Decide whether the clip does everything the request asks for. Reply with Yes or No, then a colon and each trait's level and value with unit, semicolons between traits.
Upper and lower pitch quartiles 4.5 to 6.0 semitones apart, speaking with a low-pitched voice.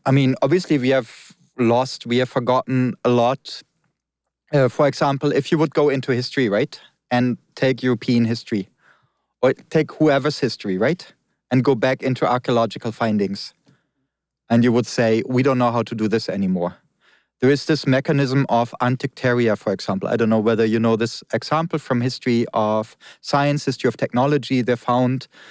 No: average, 2.9 semitones; low, 125 Hz